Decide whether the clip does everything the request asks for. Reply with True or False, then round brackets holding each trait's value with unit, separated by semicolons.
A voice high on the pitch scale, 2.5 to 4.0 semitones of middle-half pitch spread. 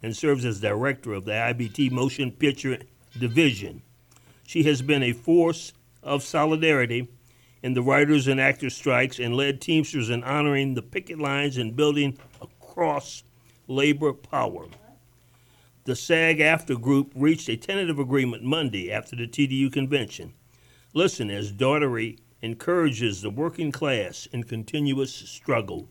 False (135 Hz; 3.2 semitones)